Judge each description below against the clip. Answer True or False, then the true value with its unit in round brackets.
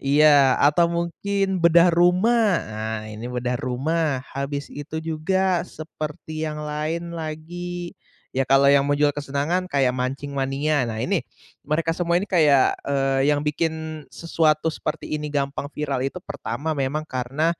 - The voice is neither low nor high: True (150 Hz)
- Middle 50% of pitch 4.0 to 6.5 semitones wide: False (3.3 semitones)